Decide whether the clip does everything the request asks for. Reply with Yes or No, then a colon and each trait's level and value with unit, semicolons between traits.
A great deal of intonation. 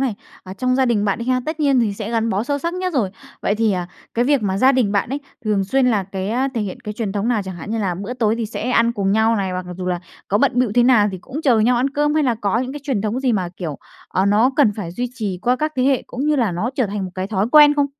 No: average, 4.4 semitones